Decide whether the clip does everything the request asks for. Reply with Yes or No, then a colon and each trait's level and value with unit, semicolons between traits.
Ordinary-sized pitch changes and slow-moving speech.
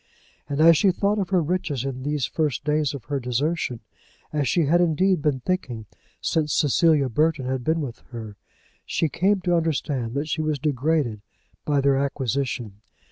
No: average, 3.8 semitones; average, 175 wpm